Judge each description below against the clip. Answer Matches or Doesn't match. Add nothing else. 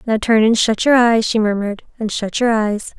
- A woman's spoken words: Matches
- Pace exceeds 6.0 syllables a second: Doesn't match